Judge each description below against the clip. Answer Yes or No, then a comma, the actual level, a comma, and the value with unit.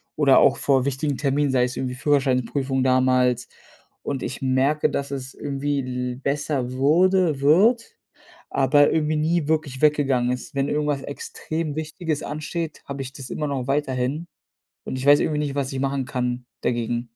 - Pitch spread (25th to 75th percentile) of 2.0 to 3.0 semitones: Yes, narrow, 2.6 semitones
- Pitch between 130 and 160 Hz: Yes, medium, 140 Hz